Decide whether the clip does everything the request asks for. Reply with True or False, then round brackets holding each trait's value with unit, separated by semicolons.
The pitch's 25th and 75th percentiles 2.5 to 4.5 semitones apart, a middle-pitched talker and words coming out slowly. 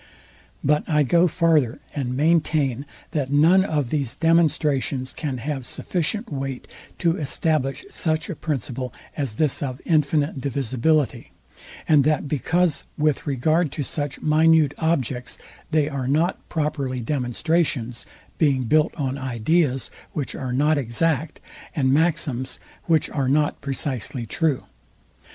True (3.3 semitones; 145 Hz; 130 wpm)